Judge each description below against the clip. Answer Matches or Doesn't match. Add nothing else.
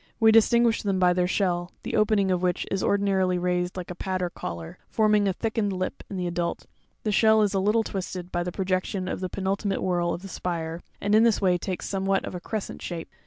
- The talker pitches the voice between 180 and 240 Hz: Matches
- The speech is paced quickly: Matches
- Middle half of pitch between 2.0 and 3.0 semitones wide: Matches